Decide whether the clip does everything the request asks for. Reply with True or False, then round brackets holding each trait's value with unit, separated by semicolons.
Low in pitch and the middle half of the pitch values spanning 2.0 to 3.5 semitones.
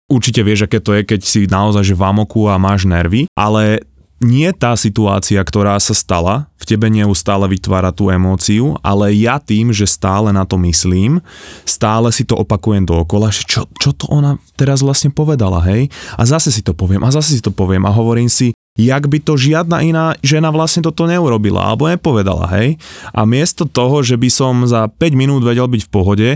False (110 Hz; 5.4 semitones)